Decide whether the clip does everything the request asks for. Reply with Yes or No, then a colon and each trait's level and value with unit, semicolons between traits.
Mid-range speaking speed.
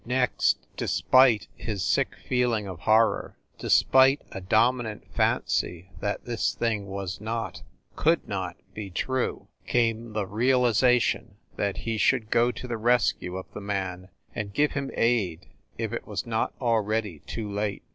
Yes: average, 145 wpm